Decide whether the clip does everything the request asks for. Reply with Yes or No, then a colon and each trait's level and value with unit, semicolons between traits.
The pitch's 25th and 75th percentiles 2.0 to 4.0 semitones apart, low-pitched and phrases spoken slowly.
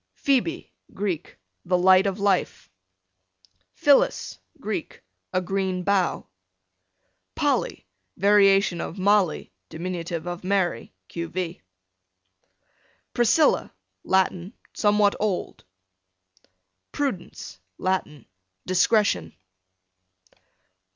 No: narrow, 2.5 semitones; high, 190 Hz; slow, 75 wpm